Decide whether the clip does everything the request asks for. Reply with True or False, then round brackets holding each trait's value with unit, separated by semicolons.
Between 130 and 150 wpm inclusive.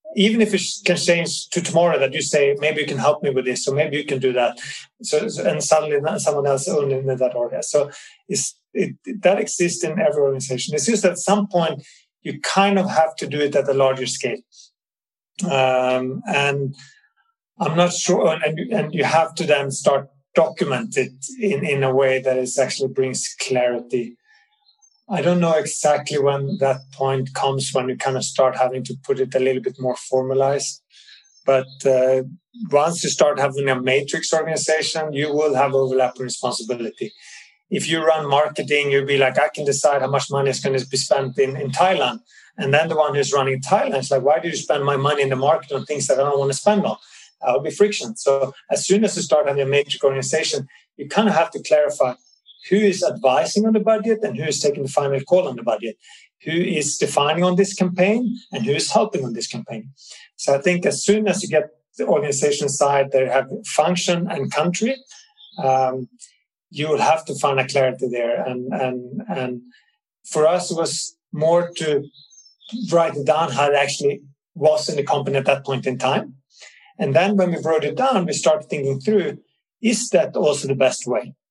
False (205 wpm)